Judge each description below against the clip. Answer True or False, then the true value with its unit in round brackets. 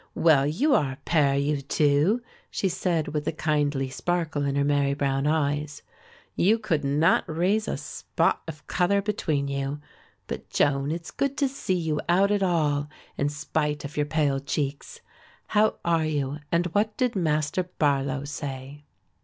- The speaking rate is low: False (165 wpm)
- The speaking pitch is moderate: True (150 Hz)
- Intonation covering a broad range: False (3.7 semitones)